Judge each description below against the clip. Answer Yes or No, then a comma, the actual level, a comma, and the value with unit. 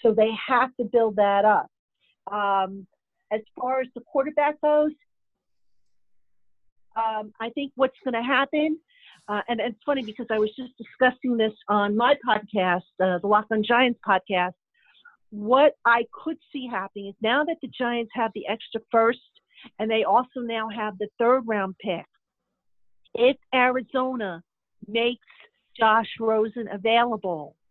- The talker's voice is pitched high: Yes, high, 225 Hz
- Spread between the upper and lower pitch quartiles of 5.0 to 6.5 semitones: No, average, 3.6 semitones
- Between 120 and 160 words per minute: Yes, average, 150 wpm